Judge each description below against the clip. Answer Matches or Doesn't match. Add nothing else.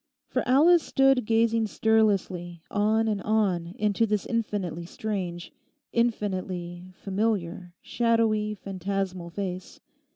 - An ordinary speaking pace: Doesn't match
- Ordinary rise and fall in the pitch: Matches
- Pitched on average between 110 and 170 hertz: Doesn't match